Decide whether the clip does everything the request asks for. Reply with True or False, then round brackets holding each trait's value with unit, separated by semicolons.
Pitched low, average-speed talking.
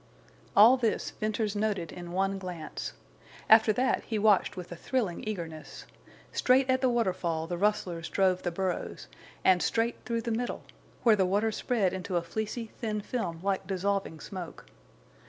False (200 Hz; 160 wpm)